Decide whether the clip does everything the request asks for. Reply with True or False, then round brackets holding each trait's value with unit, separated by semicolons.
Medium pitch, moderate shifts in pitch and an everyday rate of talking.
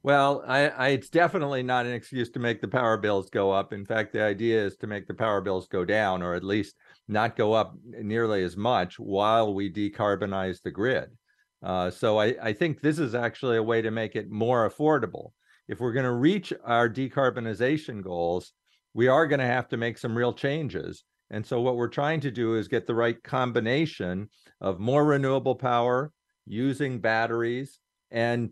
False (120 Hz; 3.9 semitones; 195 wpm)